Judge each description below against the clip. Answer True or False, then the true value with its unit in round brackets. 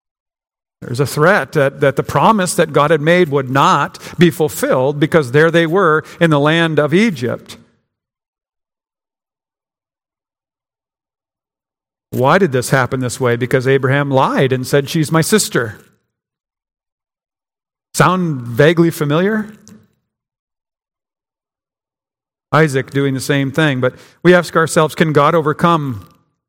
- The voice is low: False (150 Hz)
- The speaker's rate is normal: False (120 wpm)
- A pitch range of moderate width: True (3.8 semitones)